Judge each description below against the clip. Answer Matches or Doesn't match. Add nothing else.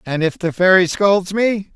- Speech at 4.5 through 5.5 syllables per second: Doesn't match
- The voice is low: Doesn't match